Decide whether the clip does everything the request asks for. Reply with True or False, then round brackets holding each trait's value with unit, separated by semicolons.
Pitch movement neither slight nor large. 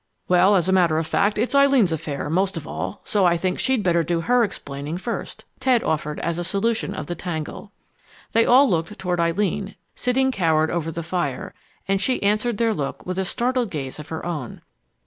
True (4.9 semitones)